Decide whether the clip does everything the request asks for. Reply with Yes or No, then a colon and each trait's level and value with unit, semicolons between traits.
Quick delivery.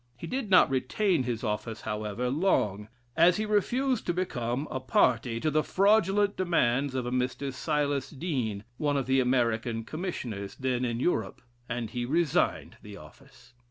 No: average, 160 wpm